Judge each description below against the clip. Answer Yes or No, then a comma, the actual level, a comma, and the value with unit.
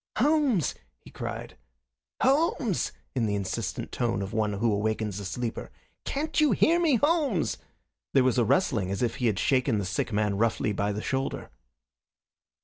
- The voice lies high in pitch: No, low, 120 Hz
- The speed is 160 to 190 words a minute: Yes, average, 165 wpm